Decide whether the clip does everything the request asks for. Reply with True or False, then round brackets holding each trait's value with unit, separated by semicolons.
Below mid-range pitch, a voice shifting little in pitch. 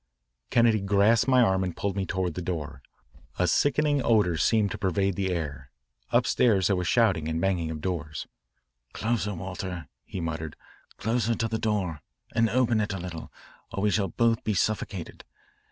False (95 Hz; 4.2 semitones)